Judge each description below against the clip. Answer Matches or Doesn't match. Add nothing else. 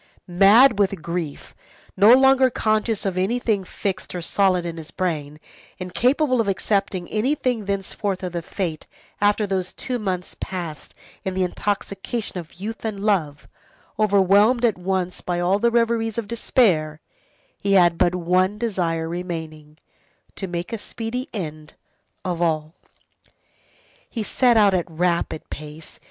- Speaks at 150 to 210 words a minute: Doesn't match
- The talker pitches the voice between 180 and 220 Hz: Matches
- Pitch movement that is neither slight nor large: Matches